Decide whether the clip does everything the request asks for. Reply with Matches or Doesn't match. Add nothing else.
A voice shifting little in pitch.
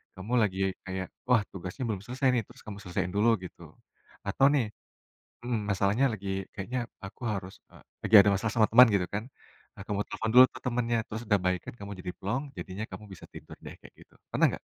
Doesn't match